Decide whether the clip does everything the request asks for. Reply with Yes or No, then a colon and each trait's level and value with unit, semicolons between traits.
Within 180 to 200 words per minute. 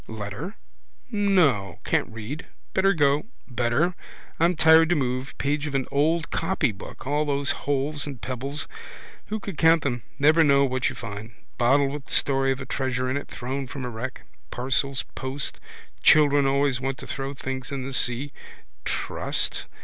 No: average, 165 wpm